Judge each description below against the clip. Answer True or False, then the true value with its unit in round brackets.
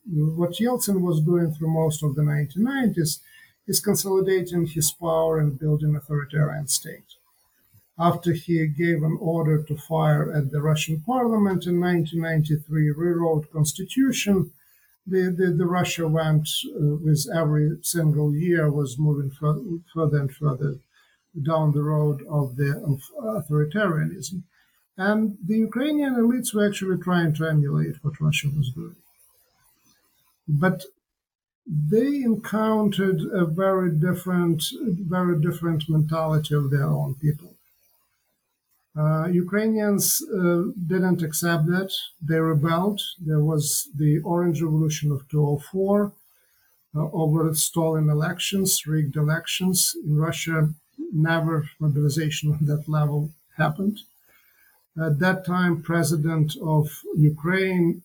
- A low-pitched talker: False (165 Hz)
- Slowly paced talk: True (120 wpm)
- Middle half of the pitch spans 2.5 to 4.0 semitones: True (3.4 semitones)